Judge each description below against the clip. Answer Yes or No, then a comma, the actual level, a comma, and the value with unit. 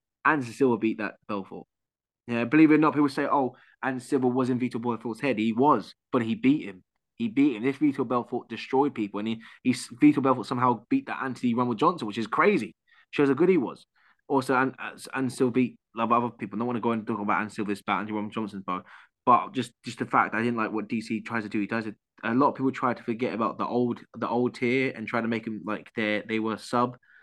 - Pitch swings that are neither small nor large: Yes, average, 3.0 semitones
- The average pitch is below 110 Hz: No, low, 120 Hz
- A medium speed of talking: No, fast, 255 wpm